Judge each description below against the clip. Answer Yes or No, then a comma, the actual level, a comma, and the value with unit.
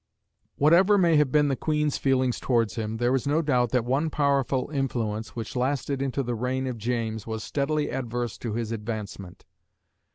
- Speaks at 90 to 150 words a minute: No, average, 175 wpm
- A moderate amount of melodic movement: Yes, average, 3.7 semitones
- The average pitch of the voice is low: Yes, low, 125 Hz